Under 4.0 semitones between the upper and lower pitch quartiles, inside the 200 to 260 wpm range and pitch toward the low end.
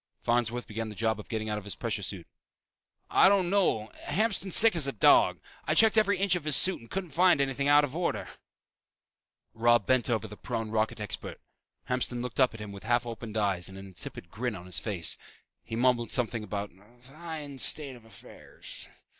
No: average, 5.3 semitones; fast, 205 wpm; low, 120 Hz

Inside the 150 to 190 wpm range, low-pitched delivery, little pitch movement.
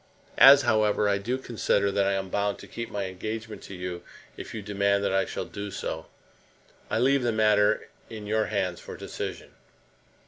Yes: average, 185 wpm; low, 105 Hz; narrow, 1.9 semitones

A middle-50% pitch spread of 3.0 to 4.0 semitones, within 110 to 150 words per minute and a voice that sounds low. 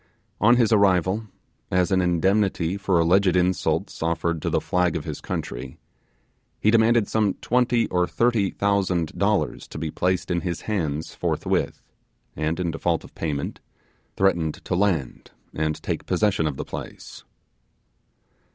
Yes: average, 3.7 semitones; average, 145 wpm; very low, 90 Hz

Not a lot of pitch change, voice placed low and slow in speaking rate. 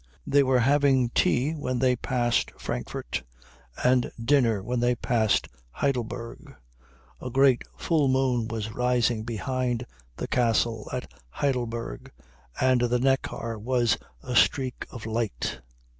Yes: narrow, 2.0 semitones; low, 125 Hz; slow, 125 wpm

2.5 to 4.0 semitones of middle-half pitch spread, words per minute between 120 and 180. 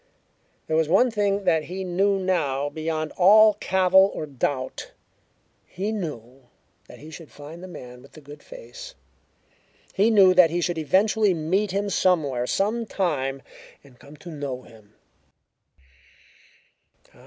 No: average, 5.3 semitones; average, 140 wpm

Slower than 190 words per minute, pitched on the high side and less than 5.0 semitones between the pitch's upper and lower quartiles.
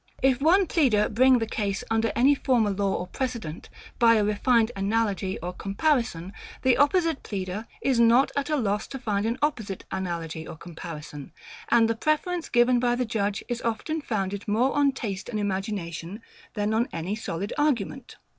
Yes: average, 175 wpm; high, 225 Hz; average, 4.5 semitones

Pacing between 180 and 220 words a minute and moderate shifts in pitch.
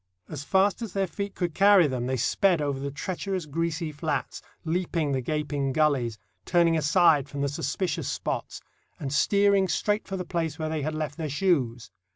Yes: average, 185 wpm; average, 4.5 semitones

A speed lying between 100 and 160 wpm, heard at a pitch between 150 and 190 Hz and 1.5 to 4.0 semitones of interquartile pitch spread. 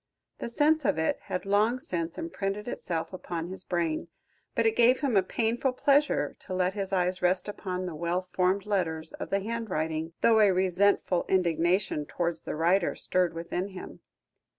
No: average, 175 wpm; medium, 185 Hz; average, 3.4 semitones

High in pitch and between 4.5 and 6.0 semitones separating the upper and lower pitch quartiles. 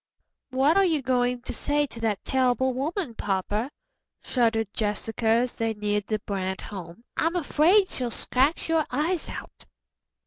Yes: high, 245 Hz; average, 5.2 semitones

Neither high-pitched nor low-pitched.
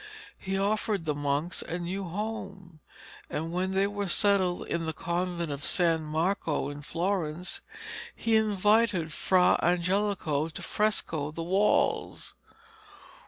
Yes: medium, 180 Hz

